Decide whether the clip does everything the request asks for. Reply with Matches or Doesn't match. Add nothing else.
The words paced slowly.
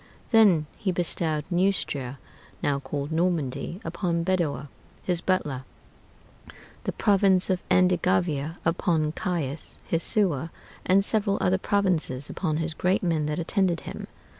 Matches